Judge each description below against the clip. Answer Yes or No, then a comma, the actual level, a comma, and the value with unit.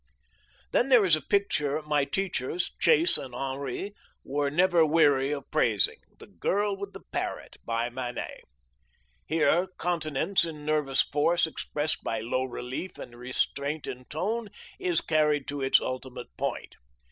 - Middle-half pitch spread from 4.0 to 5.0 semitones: Yes, average, 4.7 semitones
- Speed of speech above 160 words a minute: No, average, 145 wpm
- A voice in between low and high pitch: Yes, medium, 150 Hz